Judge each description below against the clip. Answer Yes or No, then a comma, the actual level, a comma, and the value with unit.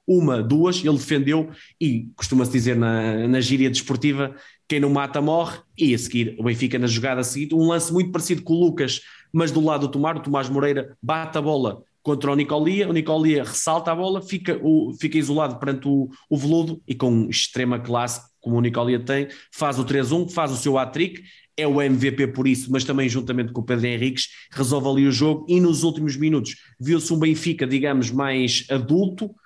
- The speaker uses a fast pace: Yes, fast, 200 wpm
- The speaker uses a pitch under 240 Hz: Yes, medium, 140 Hz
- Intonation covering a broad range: No, average, 3.5 semitones